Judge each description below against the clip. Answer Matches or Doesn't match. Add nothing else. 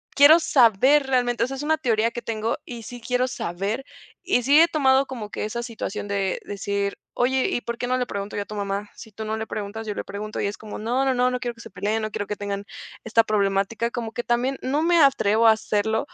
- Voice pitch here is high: Matches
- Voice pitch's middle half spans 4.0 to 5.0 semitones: Doesn't match